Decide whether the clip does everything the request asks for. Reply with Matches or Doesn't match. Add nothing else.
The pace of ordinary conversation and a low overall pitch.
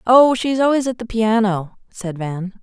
Doesn't match